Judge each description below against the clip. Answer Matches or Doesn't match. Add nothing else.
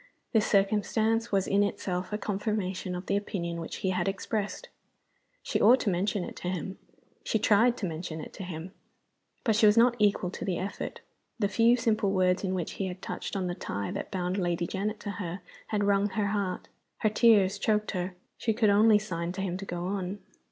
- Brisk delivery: Matches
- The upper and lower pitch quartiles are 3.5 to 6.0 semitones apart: Doesn't match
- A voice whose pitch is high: Matches